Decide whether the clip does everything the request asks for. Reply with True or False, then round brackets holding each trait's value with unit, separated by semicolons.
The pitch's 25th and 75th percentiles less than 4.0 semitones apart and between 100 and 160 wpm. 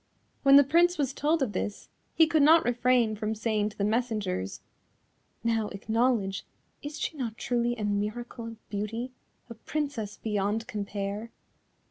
True (3.6 semitones; 150 wpm)